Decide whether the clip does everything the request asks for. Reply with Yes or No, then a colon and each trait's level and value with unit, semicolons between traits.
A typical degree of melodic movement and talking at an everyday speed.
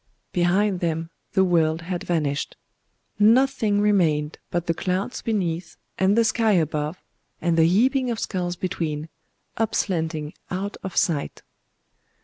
No: average, 4.0 semitones; slow, 130 wpm